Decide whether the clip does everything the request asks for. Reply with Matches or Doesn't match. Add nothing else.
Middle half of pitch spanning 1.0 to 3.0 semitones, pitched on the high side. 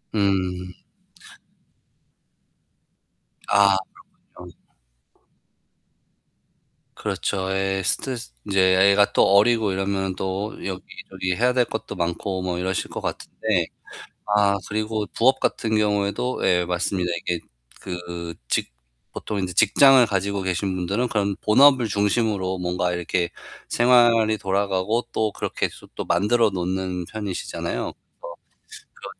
Doesn't match